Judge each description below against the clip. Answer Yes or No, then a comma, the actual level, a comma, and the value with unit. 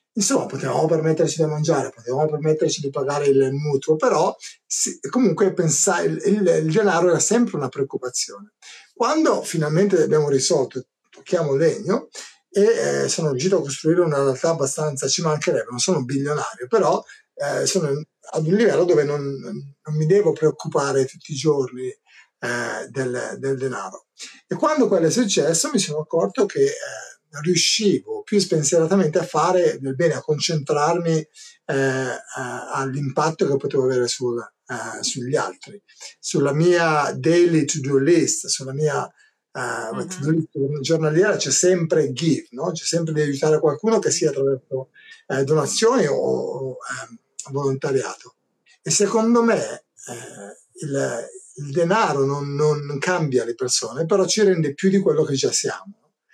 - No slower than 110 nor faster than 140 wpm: No, average, 150 wpm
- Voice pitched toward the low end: No, medium, 155 Hz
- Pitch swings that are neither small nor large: Yes, average, 5.0 semitones